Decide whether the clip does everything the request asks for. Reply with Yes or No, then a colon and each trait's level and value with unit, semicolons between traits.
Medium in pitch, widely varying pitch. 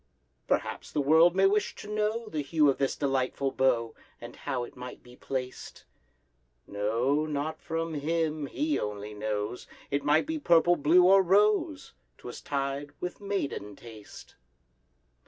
Yes: medium, 145 Hz; wide, 5.7 semitones